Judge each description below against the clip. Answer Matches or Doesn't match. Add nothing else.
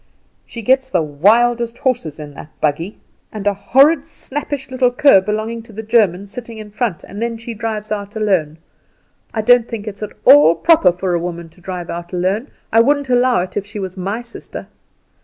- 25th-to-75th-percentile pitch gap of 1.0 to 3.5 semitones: Doesn't match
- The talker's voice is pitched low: Doesn't match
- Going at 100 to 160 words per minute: Doesn't match